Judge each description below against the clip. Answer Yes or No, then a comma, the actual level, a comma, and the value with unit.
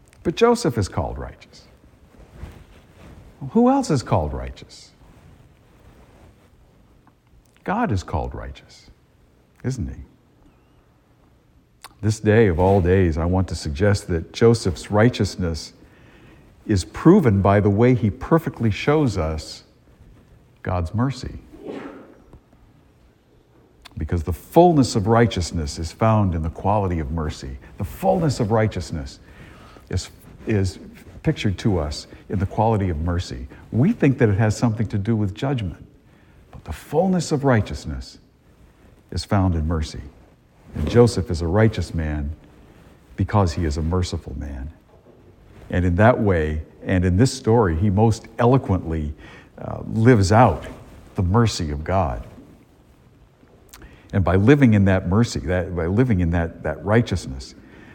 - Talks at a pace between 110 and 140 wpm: Yes, slow, 135 wpm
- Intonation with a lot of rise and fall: Yes, wide, 5.8 semitones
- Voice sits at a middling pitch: No, very low, 95 Hz